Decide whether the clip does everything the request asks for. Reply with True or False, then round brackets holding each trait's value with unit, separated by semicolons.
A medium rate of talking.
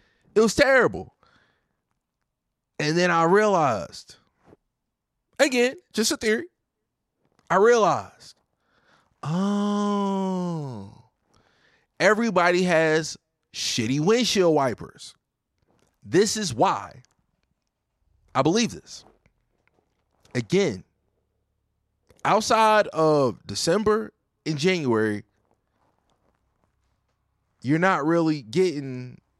False (70 wpm)